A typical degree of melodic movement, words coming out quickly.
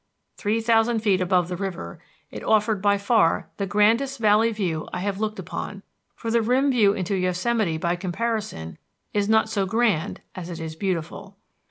No: average, 3.5 semitones; average, 175 wpm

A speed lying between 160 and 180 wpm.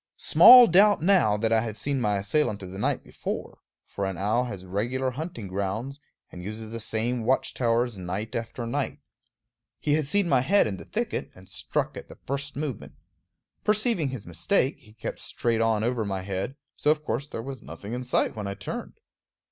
No: average, 195 wpm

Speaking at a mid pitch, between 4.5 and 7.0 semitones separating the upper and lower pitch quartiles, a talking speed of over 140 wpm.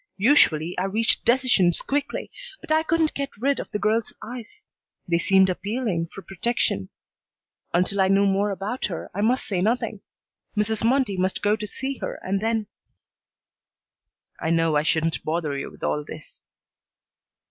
No: high, 200 Hz; average, 5.1 semitones; average, 160 wpm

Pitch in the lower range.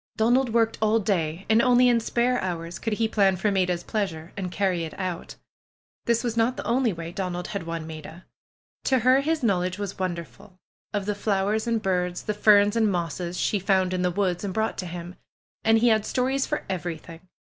No: high, 195 Hz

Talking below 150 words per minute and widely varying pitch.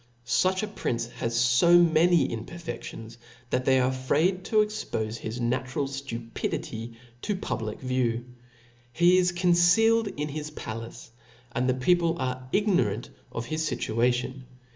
Yes: slow, 135 wpm; wide, 6.6 semitones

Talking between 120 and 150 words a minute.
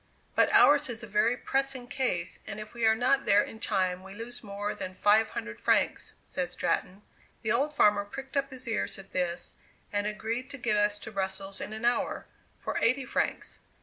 No: average, 200 wpm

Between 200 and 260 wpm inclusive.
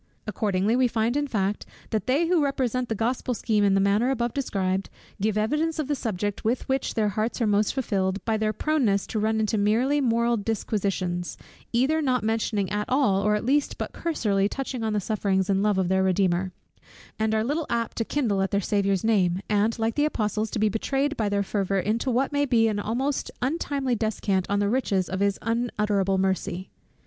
Yes: fast, 205 wpm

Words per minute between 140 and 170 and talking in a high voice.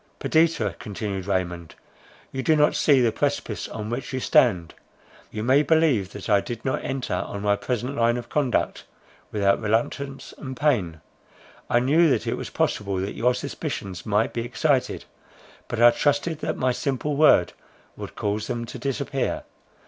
No: average, 165 wpm; low, 120 Hz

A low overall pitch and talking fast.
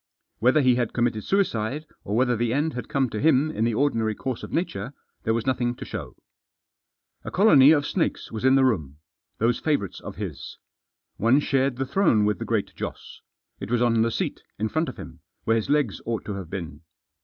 Yes: low, 120 Hz; fast, 210 wpm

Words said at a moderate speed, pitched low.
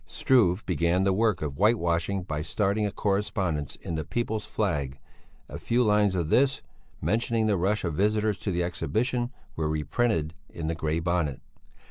Yes: average, 165 wpm; very low, 95 Hz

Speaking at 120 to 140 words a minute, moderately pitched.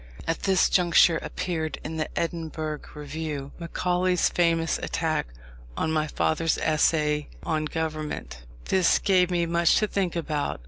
Yes: slow, 135 wpm; medium, 160 Hz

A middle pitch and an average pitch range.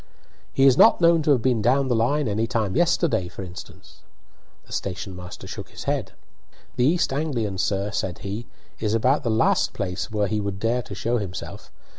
No: low, 115 Hz; average, 5.0 semitones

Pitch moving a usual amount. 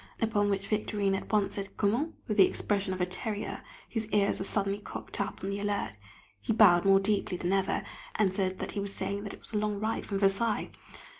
No: narrow, 1.5 semitones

